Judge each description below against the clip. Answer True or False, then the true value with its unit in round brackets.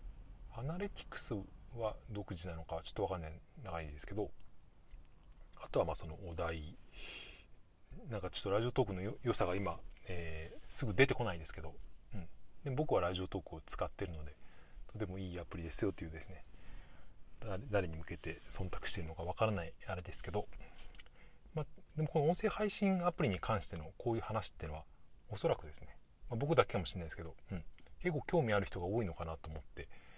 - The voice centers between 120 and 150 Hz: False (95 Hz)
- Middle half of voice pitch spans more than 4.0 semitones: True (5.3 semitones)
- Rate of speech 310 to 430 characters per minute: True (370 characters per minute)